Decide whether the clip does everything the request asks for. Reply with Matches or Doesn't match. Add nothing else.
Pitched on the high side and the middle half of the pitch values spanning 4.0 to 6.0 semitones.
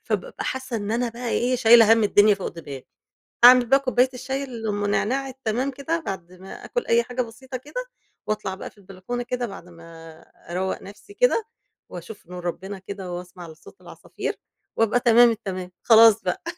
Matches